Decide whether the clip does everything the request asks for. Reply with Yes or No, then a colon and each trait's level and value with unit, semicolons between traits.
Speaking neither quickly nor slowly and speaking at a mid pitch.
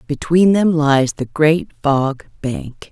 Yes: average, 145 wpm; medium, 150 Hz